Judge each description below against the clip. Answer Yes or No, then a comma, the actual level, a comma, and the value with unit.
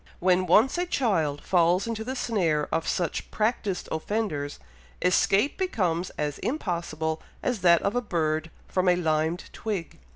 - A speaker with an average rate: Yes, average, 150 wpm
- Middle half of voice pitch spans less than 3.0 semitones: No, average, 5.3 semitones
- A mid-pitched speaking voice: Yes, medium, 180 Hz